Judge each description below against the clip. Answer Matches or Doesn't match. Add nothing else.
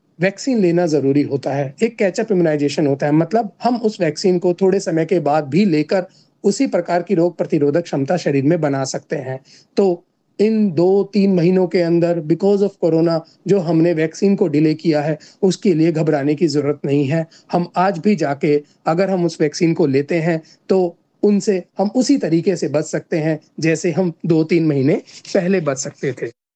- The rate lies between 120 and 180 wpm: Doesn't match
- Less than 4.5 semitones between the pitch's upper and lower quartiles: Matches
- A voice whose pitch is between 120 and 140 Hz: Doesn't match